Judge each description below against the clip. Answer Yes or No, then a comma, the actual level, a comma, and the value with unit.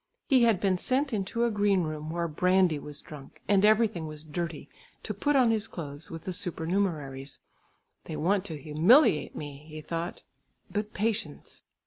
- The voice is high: No, medium, 175 Hz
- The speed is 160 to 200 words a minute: Yes, average, 165 wpm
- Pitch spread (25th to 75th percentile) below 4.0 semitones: No, average, 5.2 semitones